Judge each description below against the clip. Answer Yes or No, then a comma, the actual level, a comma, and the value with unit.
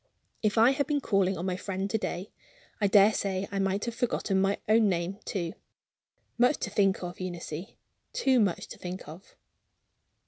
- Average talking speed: Yes, average, 170 wpm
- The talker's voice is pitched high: Yes, high, 195 Hz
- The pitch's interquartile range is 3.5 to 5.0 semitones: No, average, 3.0 semitones